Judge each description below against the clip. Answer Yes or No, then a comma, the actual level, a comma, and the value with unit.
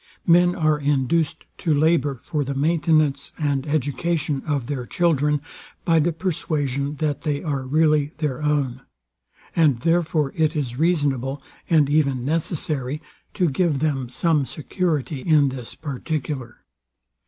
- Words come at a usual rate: No, slow, 130 wpm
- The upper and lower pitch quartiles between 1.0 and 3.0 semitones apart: Yes, average, 2.7 semitones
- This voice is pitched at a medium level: Yes, medium, 150 Hz